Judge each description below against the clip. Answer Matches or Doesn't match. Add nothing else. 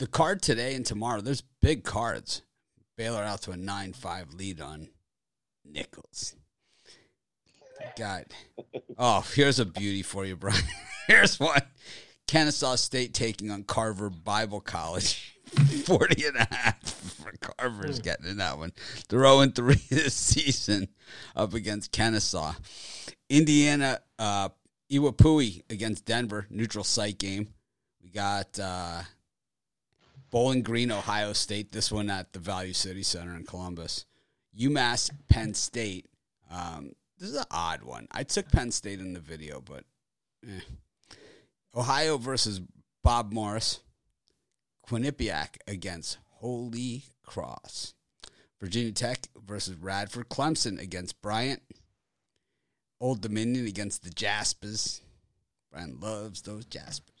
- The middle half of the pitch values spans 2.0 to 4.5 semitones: Matches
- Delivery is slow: Matches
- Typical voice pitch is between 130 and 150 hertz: Doesn't match